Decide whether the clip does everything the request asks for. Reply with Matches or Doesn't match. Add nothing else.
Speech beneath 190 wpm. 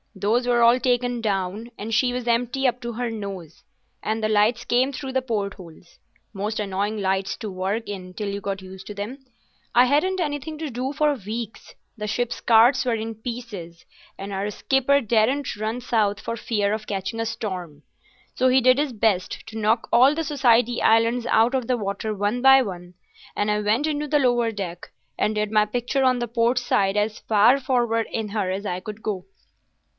Doesn't match